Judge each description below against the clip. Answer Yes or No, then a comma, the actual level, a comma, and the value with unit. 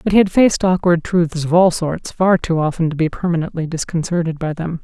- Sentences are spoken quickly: Yes, fast, 225 wpm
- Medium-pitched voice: Yes, medium, 170 Hz